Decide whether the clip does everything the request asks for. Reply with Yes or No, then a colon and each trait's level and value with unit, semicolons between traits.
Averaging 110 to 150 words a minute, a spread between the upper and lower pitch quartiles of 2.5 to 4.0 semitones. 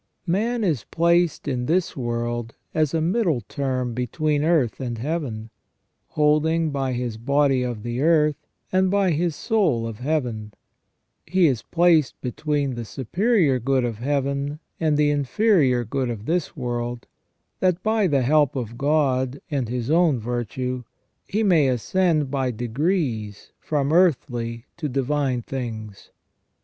No: average, 140 wpm; average, 4.8 semitones